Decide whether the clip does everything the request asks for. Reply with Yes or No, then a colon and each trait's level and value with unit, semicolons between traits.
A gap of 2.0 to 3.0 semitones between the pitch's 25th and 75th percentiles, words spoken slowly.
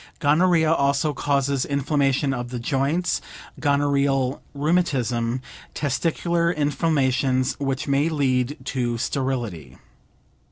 Yes: narrow, 2.5 semitones; slow, 90 wpm